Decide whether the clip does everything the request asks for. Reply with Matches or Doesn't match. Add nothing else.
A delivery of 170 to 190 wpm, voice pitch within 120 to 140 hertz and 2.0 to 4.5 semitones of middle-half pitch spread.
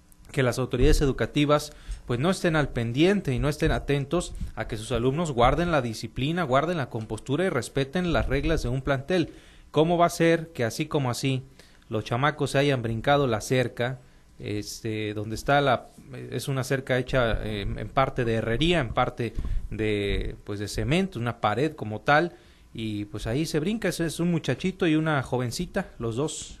Doesn't match